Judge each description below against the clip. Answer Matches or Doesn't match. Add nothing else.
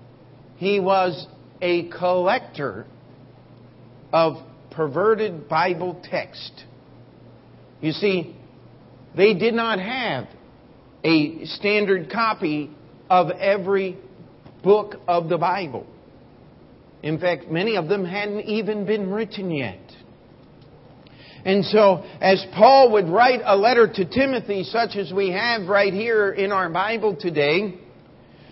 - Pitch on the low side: Doesn't match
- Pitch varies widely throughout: Doesn't match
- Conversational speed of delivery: Doesn't match